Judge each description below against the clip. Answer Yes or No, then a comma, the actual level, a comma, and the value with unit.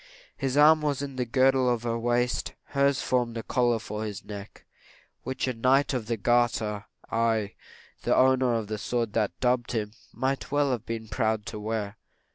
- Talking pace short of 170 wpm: No, average, 180 wpm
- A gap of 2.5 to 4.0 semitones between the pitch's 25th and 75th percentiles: Yes, average, 2.9 semitones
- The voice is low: Yes, low, 120 Hz